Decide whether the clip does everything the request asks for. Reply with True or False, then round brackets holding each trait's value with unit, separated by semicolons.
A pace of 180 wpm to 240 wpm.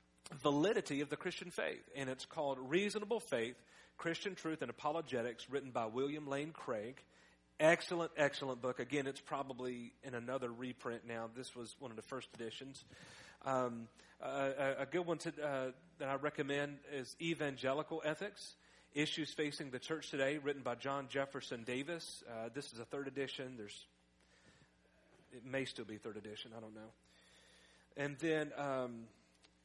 False (160 wpm)